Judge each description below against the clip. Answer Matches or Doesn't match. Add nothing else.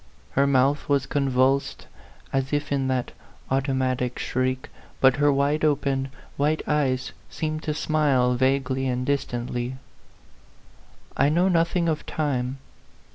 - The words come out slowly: Matches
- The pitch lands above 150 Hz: Doesn't match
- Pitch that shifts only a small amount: Matches